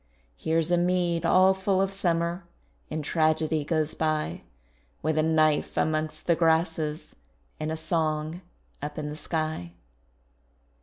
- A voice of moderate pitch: Yes, medium, 160 Hz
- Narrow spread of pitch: Yes, narrow, 1.7 semitones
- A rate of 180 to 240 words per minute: No, slow, 135 wpm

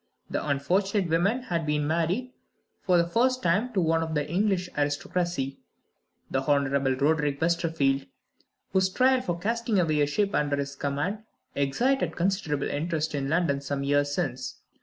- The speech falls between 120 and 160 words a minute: Yes, average, 155 wpm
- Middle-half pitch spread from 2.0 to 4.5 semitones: No, average, 4.9 semitones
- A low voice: No, medium, 160 Hz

